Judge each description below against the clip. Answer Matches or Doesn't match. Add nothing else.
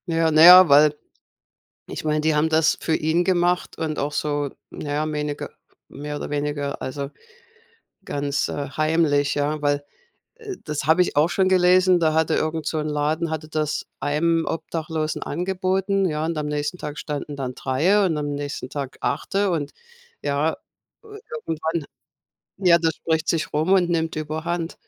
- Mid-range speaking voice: Matches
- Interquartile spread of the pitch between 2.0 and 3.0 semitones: Matches